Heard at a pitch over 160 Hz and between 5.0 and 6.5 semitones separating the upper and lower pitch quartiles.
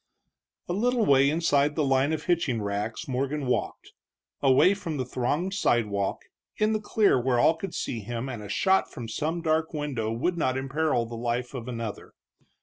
No: low, 135 Hz; average, 5.3 semitones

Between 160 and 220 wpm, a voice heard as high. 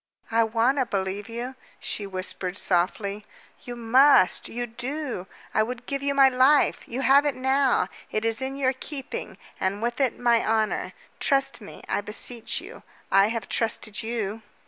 Yes: average, 170 wpm; high, 235 Hz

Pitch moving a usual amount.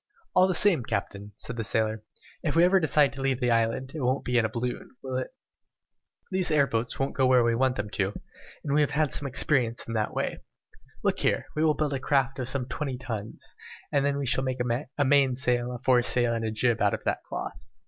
Yes: average, 3.3 semitones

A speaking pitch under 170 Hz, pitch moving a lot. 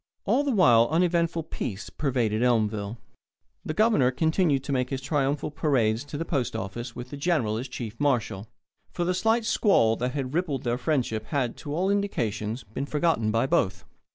Yes: low, 135 Hz; wide, 5.9 semitones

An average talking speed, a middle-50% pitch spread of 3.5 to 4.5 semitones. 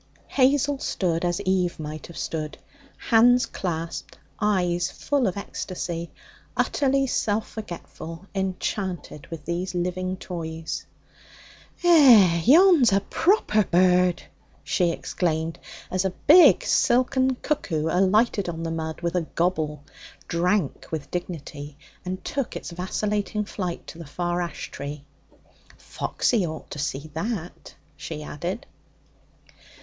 No: slow, 120 wpm; average, 4.2 semitones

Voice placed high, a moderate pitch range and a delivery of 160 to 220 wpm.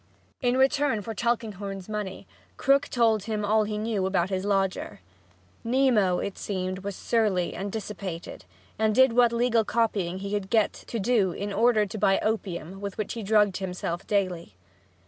Yes: high, 205 Hz; average, 3.0 semitones; average, 170 wpm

